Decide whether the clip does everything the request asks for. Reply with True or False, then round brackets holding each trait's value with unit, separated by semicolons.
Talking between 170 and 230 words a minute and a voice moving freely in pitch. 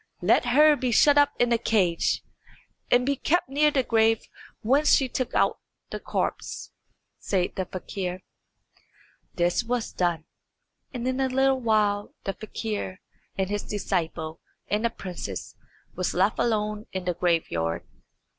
False (145 wpm; 5.7 semitones)